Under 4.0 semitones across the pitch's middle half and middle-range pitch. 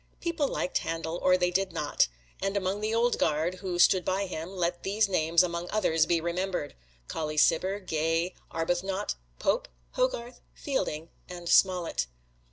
Yes: average, 3.0 semitones; medium, 180 Hz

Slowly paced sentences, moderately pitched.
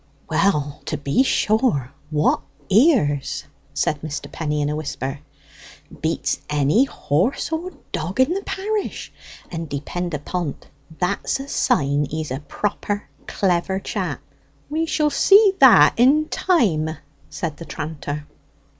Yes: slow, 130 wpm; medium, 170 Hz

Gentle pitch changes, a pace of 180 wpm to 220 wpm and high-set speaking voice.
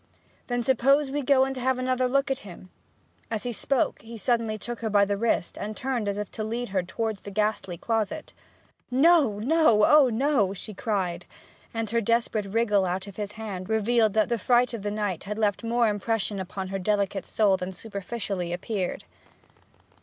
No: average, 3.2 semitones; average, 190 wpm; high, 220 Hz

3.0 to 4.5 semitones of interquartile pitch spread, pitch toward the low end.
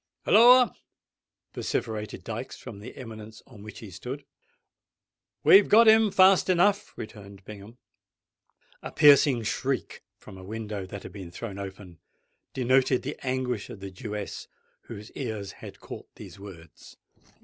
No: average, 5.3 semitones; low, 110 Hz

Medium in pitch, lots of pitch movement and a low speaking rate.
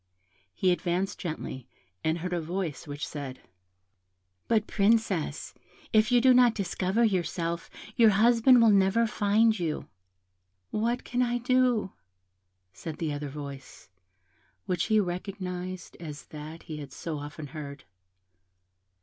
Yes: medium, 180 Hz; wide, 6.1 semitones; slow, 130 wpm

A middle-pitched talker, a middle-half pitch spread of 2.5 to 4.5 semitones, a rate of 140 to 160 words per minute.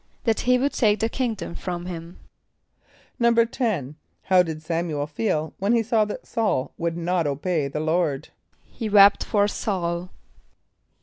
No: medium, 180 Hz; average, 5.2 semitones; average, 150 wpm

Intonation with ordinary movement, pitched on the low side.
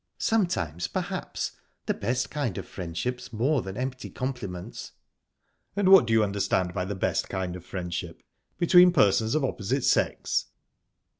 No: wide, 6.4 semitones; low, 110 Hz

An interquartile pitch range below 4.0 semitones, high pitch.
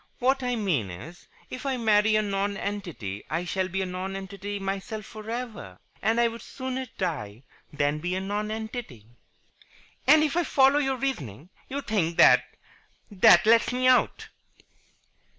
No: wide, 5.5 semitones; high, 205 Hz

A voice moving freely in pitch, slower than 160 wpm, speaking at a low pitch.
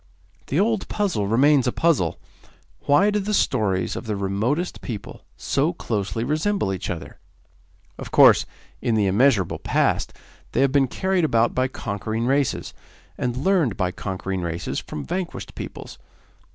Yes: wide, 7.8 semitones; average, 150 wpm; low, 125 Hz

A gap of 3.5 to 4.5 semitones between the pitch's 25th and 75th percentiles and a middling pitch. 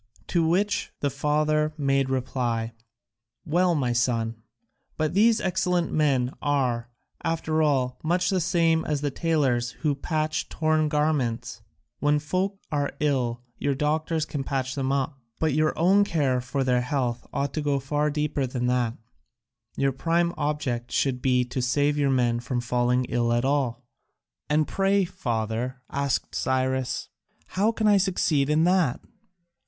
Yes: average, 3.9 semitones; medium, 145 Hz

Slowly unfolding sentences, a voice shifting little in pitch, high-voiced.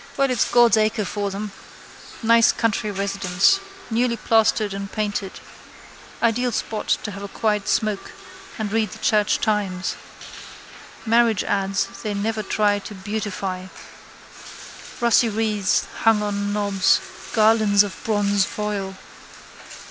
Yes: slow, 120 wpm; narrow, 1.9 semitones; high, 210 Hz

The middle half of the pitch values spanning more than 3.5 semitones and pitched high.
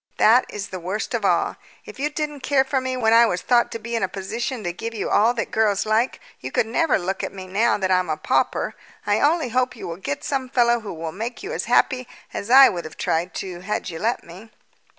Yes: average, 5.0 semitones; high, 225 Hz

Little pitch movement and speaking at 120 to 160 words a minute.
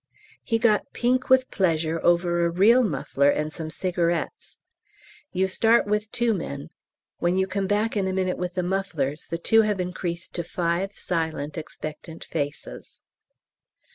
No: average, 4.0 semitones; average, 155 wpm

